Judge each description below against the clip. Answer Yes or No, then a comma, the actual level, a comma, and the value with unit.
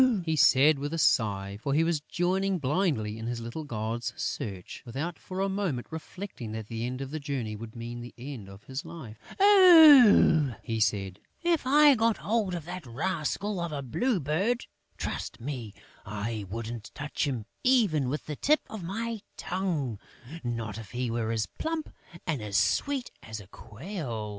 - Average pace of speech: Yes, average, 175 wpm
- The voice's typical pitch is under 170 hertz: Yes, medium, 140 Hz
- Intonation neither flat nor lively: No, wide, 8.7 semitones